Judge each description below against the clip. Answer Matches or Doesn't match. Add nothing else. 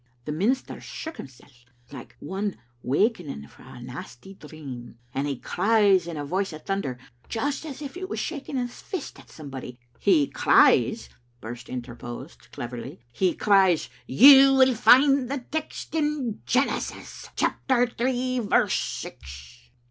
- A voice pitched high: Matches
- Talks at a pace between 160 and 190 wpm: Doesn't match